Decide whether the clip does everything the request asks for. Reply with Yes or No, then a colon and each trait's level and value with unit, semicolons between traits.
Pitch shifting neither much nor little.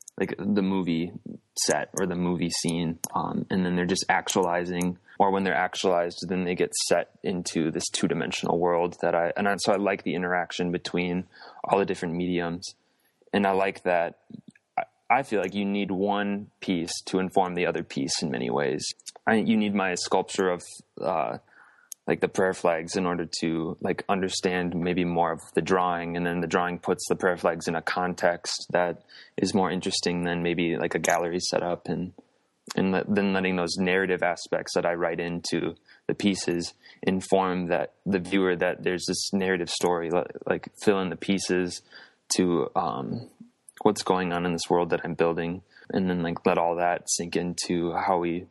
No: narrow, 1.7 semitones